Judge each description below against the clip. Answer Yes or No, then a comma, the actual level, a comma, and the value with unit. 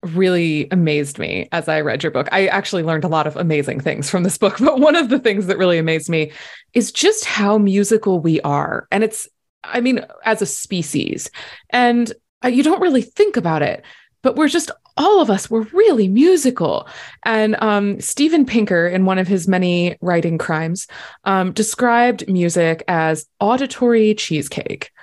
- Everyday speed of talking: Yes, average, 175 wpm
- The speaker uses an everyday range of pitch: No, wide, 6.1 semitones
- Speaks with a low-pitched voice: No, high, 195 Hz